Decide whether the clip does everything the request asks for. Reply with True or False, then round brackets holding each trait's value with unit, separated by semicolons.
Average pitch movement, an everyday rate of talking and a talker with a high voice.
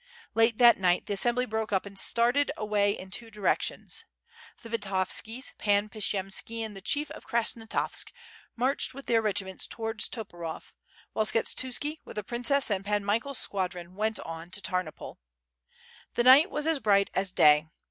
True (3.5 semitones; 160 wpm; 215 Hz)